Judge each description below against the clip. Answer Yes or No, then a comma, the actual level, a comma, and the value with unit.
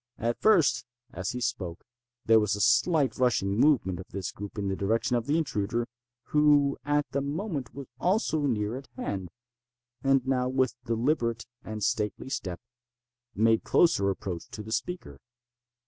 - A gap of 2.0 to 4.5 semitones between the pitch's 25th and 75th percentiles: No, wide, 5.5 semitones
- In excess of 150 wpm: Yes, average, 160 wpm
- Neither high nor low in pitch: No, low, 120 Hz